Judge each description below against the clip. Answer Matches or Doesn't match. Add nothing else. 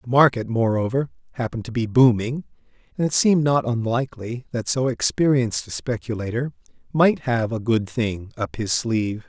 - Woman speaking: Doesn't match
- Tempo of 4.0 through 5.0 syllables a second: Doesn't match